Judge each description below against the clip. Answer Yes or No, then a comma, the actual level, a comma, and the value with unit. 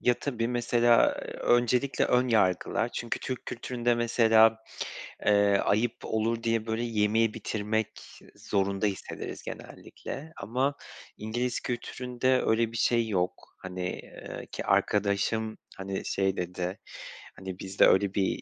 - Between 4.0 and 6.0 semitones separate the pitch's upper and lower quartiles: No, average, 3.2 semitones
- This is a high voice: No, low, 110 Hz